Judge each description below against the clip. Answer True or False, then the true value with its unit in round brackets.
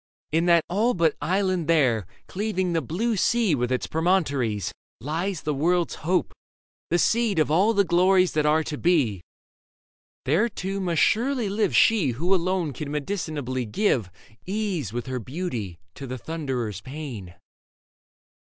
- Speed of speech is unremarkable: True (150 wpm)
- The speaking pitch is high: False (165 Hz)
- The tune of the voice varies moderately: False (6.1 semitones)